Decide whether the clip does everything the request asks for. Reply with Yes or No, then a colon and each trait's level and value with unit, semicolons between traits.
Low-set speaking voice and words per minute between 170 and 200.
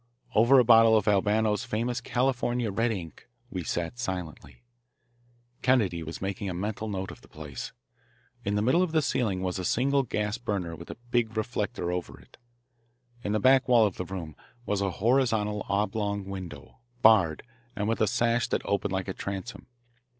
Yes: low, 105 Hz; average, 180 wpm